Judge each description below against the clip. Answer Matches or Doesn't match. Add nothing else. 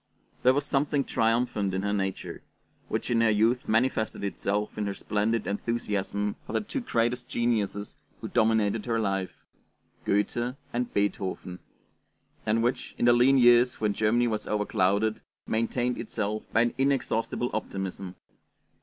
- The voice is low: Matches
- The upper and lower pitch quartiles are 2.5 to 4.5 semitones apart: Matches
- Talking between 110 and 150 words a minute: Matches